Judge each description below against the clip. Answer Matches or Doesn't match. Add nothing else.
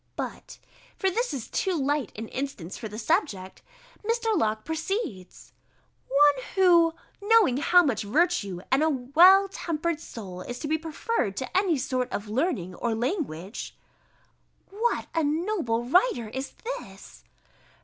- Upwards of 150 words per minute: Doesn't match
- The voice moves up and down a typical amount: Doesn't match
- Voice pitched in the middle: Doesn't match